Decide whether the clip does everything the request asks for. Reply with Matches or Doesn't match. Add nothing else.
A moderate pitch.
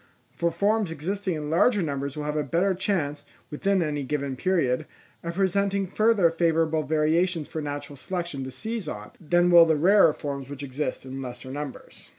Matches